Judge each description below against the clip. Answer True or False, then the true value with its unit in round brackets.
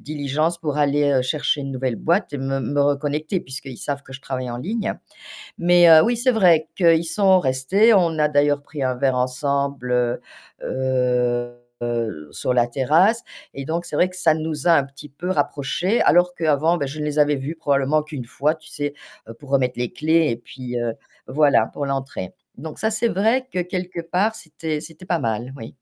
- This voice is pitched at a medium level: True (145 Hz)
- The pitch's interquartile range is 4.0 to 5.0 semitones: True (4.3 semitones)